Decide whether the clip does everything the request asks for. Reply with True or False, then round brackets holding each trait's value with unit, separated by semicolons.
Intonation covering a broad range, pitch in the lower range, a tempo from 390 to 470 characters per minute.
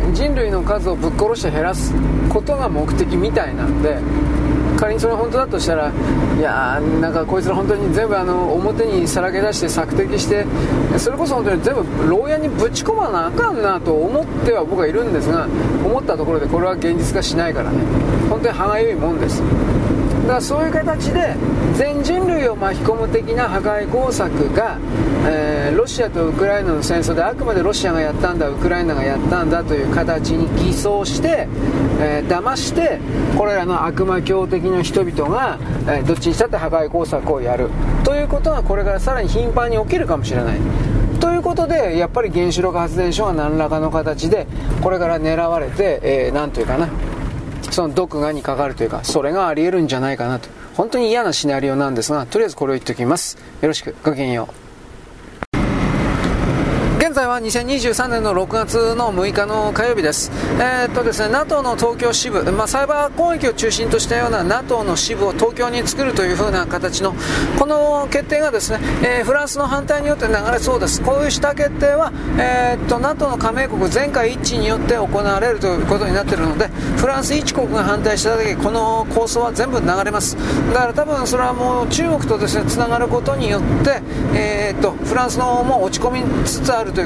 False (8.3 semitones; 215 Hz; 400 characters per minute)